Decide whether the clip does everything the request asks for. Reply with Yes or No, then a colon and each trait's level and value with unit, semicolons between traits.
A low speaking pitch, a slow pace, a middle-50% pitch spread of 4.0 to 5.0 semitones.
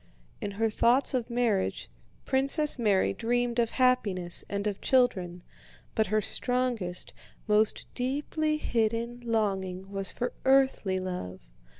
No: high, 225 Hz; slow, 120 wpm; average, 4.3 semitones